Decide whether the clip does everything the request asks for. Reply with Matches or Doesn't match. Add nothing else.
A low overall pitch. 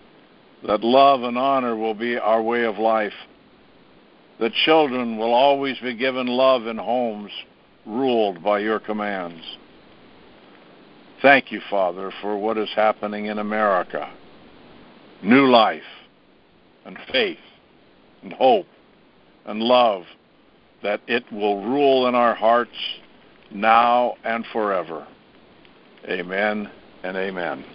Matches